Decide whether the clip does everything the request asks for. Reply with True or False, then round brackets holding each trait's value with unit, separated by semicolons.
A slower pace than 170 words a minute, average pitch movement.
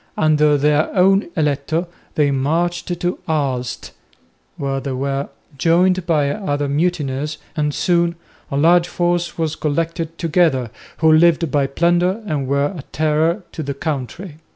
True (140 wpm; 3.3 semitones)